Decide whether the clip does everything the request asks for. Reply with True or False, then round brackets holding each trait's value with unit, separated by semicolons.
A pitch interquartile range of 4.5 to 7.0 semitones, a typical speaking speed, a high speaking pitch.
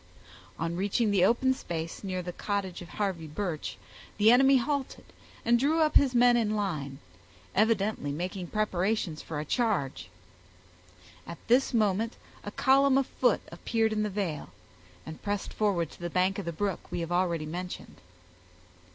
True (5.0 semitones; 160 wpm; 200 Hz)